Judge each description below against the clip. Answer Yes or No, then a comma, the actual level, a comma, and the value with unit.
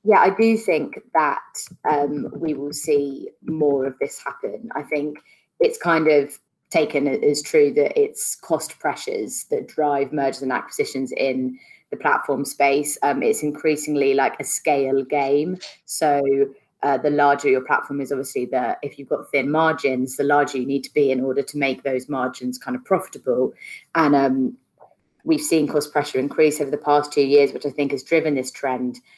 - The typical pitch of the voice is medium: Yes, medium, 145 Hz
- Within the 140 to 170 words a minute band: No, average, 185 wpm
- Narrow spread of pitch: Yes, narrow, 1.9 semitones